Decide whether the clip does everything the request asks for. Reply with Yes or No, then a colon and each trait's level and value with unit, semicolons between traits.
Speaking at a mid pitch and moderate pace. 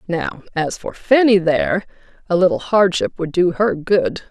Yes: medium, 180 Hz; average, 165 wpm